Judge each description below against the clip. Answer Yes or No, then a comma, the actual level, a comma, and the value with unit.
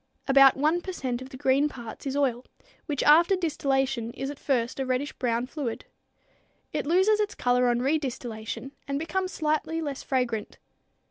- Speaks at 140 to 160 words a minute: No, average, 170 wpm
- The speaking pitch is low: No, very high, 270 Hz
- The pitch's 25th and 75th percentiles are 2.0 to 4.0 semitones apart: Yes, average, 3.6 semitones